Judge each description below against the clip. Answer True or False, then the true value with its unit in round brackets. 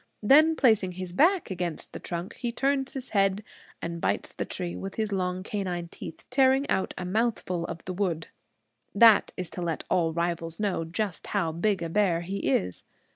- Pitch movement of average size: True (4.1 semitones)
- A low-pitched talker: False (185 Hz)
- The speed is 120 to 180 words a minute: False (190 wpm)